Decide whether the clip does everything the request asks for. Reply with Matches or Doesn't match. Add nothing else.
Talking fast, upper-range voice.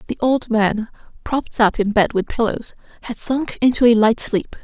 Doesn't match